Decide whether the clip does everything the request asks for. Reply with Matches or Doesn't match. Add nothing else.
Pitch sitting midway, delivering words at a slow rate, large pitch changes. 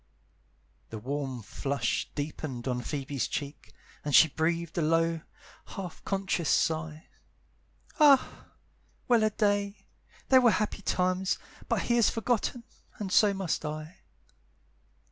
Matches